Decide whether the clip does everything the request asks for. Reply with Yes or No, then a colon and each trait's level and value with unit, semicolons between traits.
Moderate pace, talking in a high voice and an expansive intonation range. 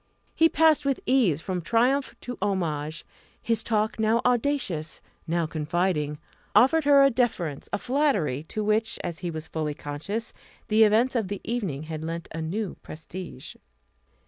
Yes: average, 155 wpm; high, 200 Hz; wide, 7.1 semitones